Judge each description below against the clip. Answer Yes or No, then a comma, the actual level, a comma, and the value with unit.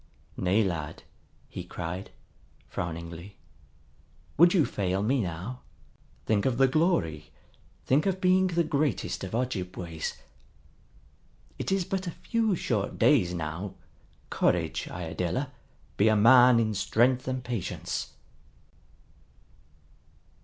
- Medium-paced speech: No, slow, 110 wpm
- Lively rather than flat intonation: Yes, wide, 7.9 semitones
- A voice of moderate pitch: No, low, 110 Hz